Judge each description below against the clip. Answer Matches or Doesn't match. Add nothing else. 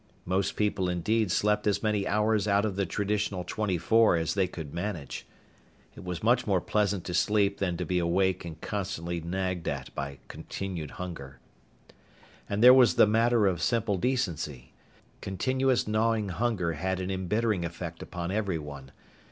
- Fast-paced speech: Doesn't match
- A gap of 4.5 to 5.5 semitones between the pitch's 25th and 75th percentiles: Doesn't match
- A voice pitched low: Matches